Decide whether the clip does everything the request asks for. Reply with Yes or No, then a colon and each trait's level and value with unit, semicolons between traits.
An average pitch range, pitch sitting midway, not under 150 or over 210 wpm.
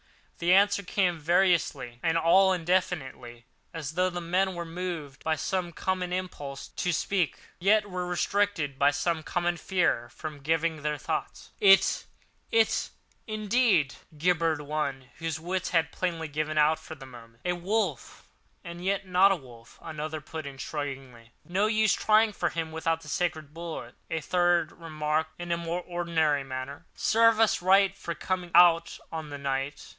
Yes: average, 3.5 semitones; medium, 165 Hz; average, 155 wpm